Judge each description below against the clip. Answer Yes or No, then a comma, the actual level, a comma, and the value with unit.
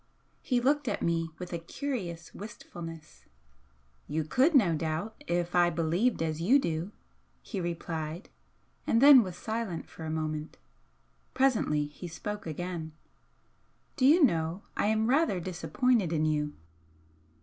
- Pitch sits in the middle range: Yes, medium, 175 Hz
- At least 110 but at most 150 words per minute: Yes, average, 140 wpm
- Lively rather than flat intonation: Yes, wide, 6.2 semitones